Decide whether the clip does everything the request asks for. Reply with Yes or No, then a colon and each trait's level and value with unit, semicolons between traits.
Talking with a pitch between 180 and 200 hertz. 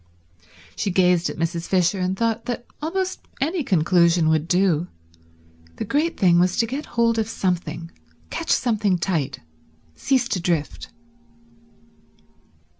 Yes: medium, 185 Hz